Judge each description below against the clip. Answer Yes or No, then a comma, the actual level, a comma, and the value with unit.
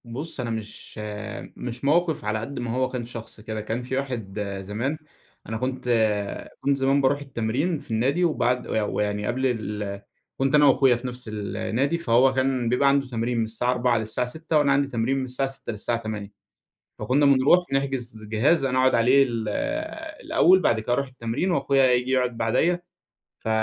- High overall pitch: No, low, 125 Hz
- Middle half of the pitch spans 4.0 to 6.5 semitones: No, average, 3.3 semitones